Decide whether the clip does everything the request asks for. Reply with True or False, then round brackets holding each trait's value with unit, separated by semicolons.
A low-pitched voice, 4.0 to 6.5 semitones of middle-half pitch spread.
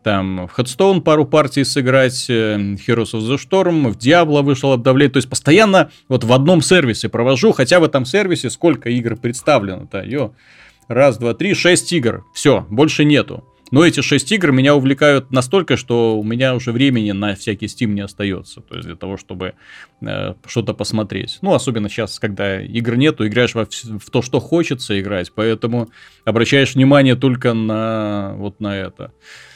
True (125 Hz; 4.7 semitones)